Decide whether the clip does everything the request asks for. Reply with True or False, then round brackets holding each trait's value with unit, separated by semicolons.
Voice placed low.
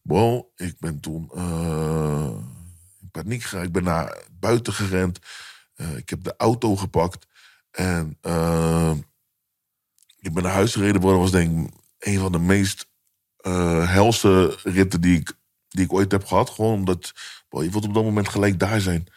True (95 Hz)